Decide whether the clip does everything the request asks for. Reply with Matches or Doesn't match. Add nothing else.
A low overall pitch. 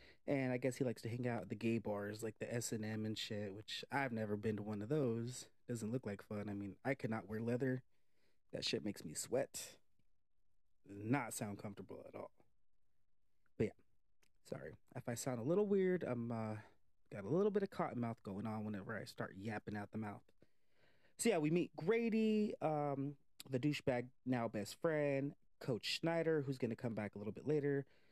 Matches